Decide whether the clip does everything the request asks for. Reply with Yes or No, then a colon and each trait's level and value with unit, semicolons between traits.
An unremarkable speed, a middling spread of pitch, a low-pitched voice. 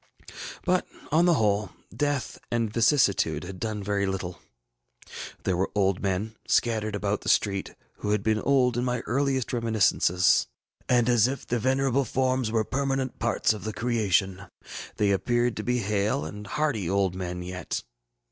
Yes: average, 160 wpm; average, 4.0 semitones; low, 110 Hz